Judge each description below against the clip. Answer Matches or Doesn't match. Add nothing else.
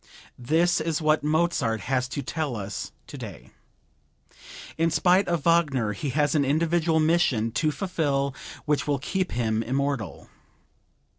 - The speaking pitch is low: Doesn't match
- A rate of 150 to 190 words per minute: Doesn't match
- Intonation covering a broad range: Doesn't match